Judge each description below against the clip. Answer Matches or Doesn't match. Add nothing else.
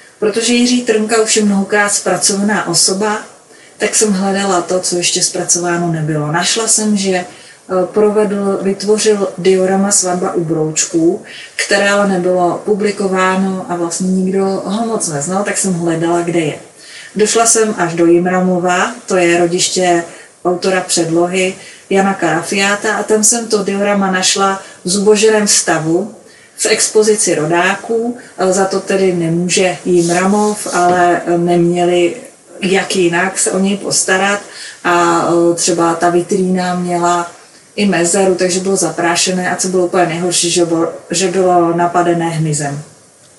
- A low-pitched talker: Doesn't match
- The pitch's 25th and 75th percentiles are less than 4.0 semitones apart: Matches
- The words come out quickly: Doesn't match